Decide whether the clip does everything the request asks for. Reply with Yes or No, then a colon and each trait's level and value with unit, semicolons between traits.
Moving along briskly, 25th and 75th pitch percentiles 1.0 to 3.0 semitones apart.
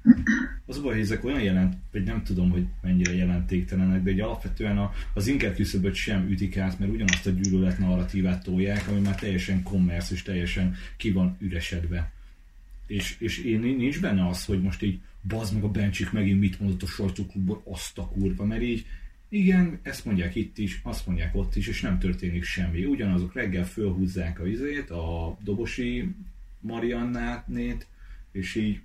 Yes: fast, 175 wpm; narrow, 2.6 semitones